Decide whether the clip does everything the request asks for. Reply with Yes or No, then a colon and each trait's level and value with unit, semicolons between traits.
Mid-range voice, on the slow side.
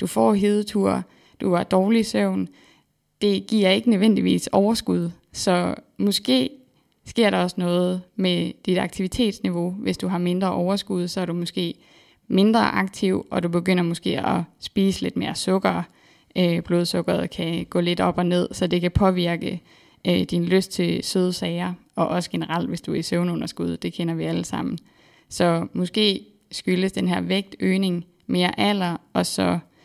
No: medium, 180 Hz; average, 160 wpm